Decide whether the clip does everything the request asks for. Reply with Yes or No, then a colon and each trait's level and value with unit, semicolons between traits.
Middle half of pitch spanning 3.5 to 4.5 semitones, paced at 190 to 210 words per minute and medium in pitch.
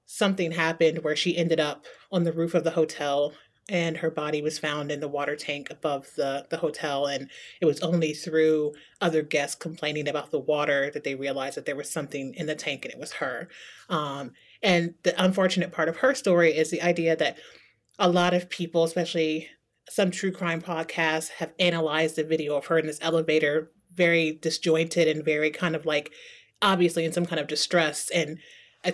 No: narrow, 2.4 semitones; average, 195 wpm; medium, 160 Hz